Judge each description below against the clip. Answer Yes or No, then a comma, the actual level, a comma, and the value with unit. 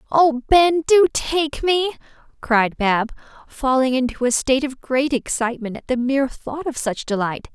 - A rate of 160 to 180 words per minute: Yes, average, 165 wpm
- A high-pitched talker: Yes, very high, 270 Hz